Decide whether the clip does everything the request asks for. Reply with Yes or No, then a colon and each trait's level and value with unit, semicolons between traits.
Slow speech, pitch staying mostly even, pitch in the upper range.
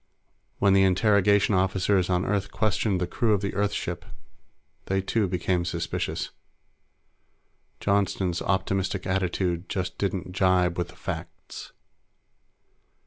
No: slow, 120 wpm; narrow, 1.7 semitones; very low, 95 Hz